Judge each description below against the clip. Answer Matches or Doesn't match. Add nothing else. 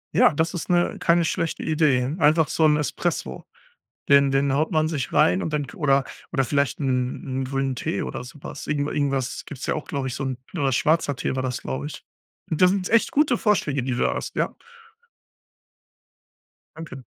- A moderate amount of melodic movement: Matches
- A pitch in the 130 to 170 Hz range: Matches